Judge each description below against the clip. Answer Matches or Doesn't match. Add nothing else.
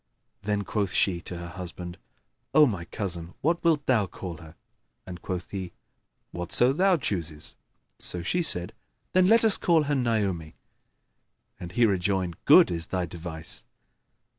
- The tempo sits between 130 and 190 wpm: Matches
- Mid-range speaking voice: Doesn't match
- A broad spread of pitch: Matches